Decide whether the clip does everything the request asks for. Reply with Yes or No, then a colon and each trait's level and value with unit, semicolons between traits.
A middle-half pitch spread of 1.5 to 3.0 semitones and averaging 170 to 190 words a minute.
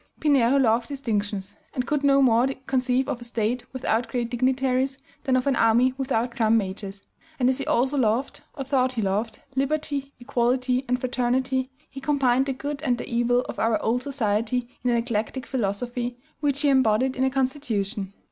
Yes: narrow, 2.4 semitones; average, 180 wpm